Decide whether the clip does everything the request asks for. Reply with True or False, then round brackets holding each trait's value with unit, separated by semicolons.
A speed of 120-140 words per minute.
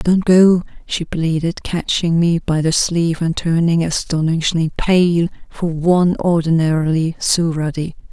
True (135 wpm)